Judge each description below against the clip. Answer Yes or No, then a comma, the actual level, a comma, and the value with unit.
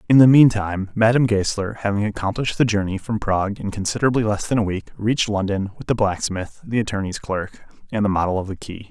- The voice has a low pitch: Yes, low, 105 Hz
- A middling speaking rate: No, fast, 210 wpm